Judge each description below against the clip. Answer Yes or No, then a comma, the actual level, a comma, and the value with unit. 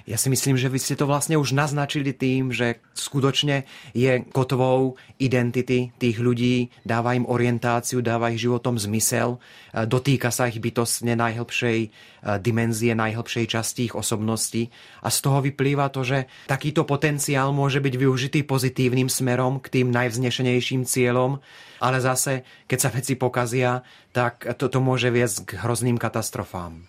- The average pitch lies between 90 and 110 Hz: No, low, 125 Hz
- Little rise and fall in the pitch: Yes, narrow, 2.0 semitones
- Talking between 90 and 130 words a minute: No, average, 145 wpm